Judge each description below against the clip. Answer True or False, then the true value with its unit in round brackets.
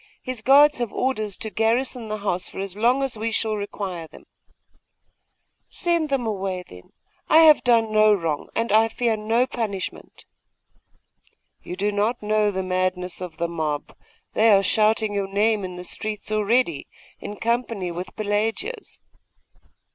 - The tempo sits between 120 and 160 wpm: True (155 wpm)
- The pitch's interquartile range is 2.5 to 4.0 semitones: True (3.4 semitones)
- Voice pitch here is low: False (215 Hz)